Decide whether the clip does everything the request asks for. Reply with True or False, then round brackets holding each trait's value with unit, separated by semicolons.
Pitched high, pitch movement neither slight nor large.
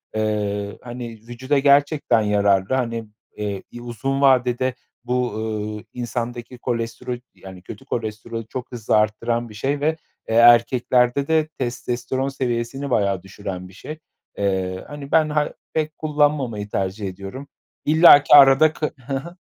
False (120 Hz; 4.3 semitones)